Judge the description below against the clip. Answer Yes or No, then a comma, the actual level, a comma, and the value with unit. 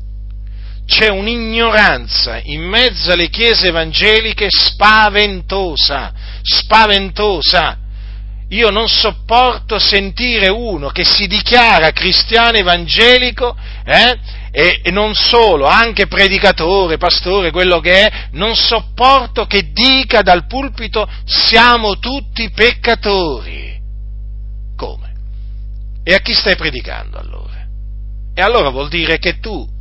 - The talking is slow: Yes, slow, 105 wpm